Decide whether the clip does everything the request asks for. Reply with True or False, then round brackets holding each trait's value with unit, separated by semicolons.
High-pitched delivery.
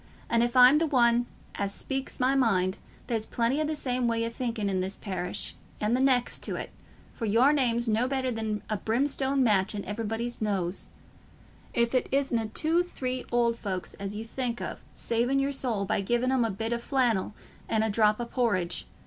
True (235 Hz)